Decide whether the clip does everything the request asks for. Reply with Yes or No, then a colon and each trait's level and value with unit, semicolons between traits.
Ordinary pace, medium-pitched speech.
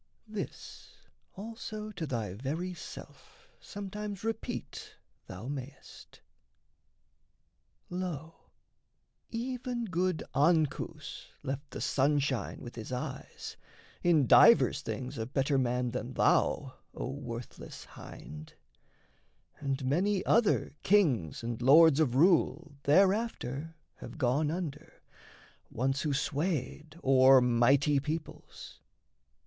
No: slow, 100 wpm; medium, 145 Hz